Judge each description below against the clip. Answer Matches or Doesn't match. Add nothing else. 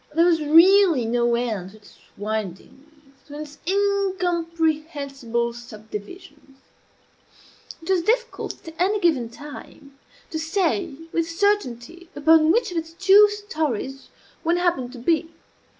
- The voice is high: Matches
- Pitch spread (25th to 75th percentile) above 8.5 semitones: Doesn't match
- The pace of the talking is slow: Matches